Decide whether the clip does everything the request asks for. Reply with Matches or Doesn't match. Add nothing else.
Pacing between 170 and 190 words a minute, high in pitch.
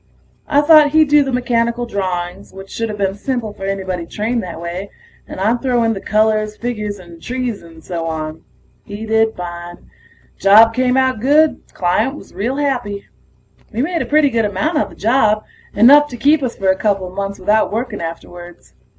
Matches